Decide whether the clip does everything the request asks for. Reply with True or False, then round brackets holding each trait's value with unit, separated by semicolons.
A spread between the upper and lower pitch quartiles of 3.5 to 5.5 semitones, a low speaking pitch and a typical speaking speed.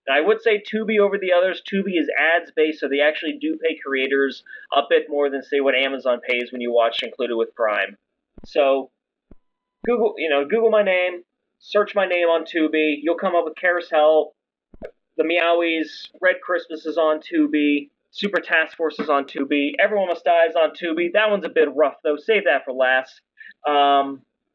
False (4.2 semitones; 160 Hz; 190 wpm)